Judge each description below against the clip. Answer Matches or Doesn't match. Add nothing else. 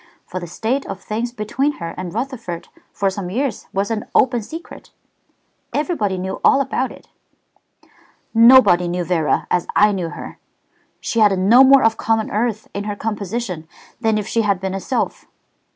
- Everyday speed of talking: Matches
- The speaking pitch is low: Doesn't match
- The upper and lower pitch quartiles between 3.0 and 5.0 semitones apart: Matches